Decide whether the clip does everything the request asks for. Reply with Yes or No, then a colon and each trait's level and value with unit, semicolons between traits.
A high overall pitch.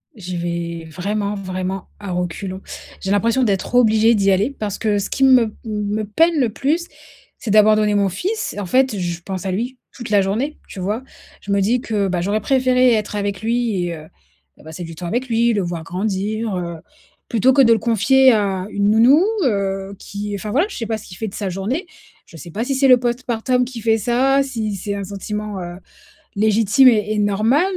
Yes: high, 210 Hz